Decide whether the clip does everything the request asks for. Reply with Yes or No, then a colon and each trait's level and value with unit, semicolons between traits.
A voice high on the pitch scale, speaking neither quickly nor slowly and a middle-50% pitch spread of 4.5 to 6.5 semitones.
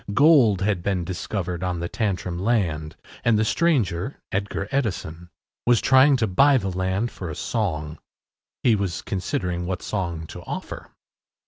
No: very low, 95 Hz; average, 150 wpm; average, 4.8 semitones